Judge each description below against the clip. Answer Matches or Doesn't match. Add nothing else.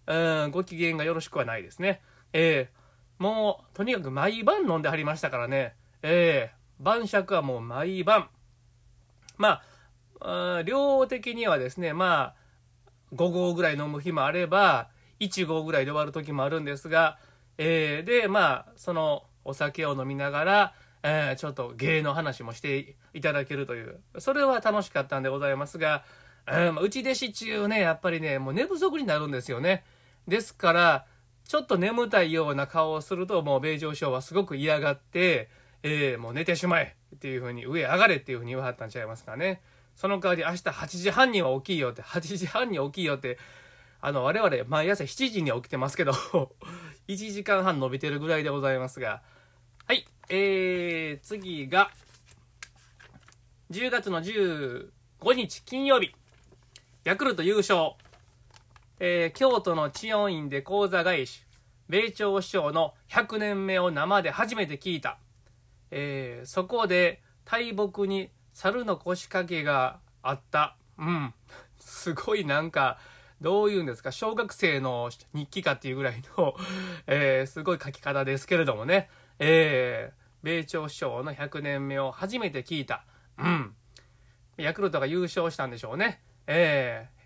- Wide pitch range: Matches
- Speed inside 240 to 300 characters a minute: Matches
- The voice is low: Doesn't match